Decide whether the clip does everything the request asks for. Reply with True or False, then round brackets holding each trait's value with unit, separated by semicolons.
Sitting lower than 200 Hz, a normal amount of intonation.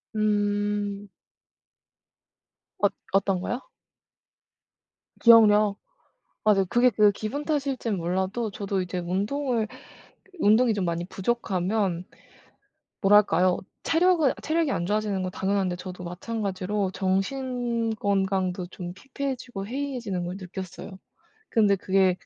False (205 Hz; 3.7 semitones)